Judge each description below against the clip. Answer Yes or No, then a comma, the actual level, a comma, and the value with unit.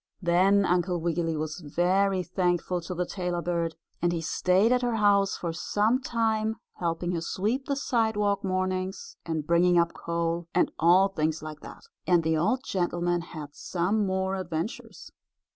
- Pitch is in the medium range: Yes, medium, 180 Hz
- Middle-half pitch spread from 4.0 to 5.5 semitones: No, average, 2.9 semitones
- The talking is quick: No, average, 160 wpm